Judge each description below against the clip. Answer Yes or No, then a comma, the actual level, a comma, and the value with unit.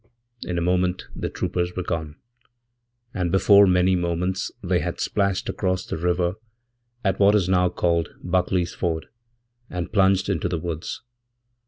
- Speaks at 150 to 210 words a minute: No, average, 140 wpm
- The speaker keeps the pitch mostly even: Yes, narrow, 1.5 semitones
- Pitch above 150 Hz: No, very low, 90 Hz